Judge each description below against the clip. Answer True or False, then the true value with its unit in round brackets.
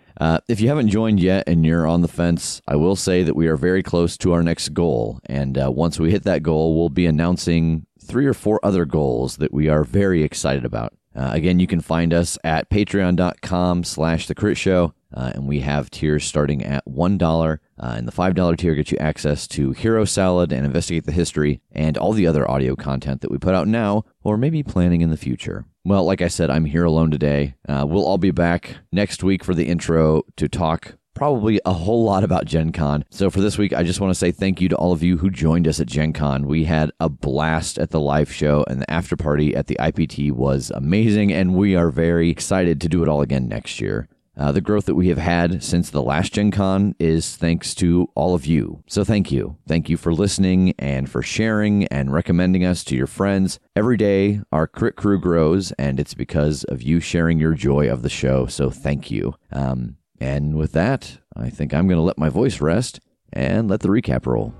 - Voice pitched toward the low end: True (85 Hz)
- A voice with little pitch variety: False (4.0 semitones)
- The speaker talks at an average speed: False (225 wpm)